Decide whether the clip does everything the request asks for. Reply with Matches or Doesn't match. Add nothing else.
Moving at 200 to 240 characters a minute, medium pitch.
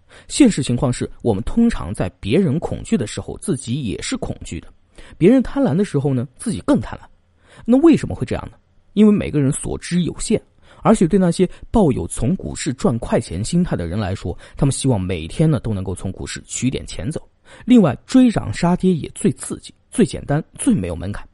Doesn't match